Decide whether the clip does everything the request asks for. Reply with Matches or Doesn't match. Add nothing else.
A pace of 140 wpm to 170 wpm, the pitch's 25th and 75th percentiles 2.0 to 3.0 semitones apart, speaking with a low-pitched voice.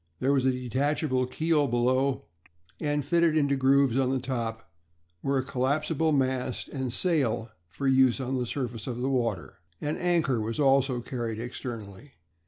Matches